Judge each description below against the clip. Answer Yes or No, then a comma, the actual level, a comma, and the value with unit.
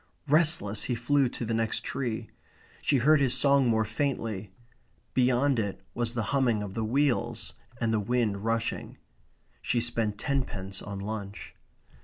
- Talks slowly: No, average, 150 wpm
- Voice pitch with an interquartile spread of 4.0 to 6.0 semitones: No, average, 3.5 semitones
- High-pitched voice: No, low, 115 Hz